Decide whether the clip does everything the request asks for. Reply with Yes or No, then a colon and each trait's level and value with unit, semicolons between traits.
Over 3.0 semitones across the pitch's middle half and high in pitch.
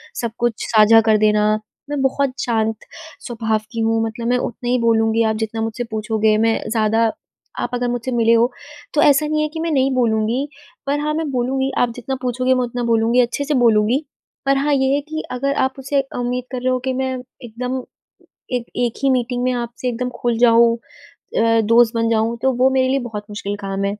No: average, 2.7 semitones; high, 240 Hz